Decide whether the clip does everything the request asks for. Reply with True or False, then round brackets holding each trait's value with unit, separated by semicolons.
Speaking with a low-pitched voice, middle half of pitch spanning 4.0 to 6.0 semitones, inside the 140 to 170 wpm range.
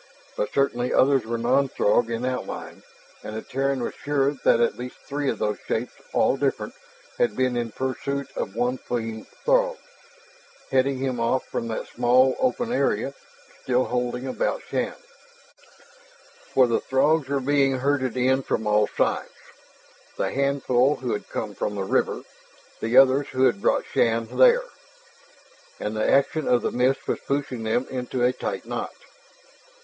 False (130 Hz; 2.7 semitones; 160 wpm)